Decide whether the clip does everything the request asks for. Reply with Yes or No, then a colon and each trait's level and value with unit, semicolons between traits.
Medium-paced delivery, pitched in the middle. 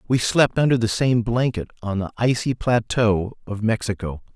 No: average, 165 wpm; low, 115 Hz